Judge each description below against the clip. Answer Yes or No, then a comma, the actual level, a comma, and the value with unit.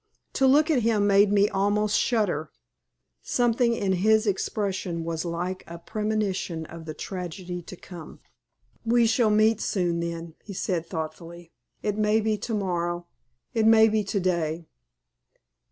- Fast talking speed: No, average, 150 wpm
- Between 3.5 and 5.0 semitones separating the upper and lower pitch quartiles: Yes, average, 4.1 semitones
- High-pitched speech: Yes, high, 195 Hz